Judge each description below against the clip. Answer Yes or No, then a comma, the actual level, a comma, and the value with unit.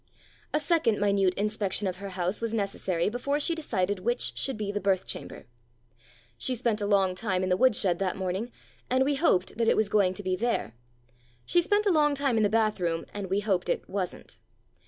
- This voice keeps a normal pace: No, fast, 215 wpm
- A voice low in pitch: No, high, 205 Hz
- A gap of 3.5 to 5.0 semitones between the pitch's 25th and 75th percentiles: Yes, average, 4.4 semitones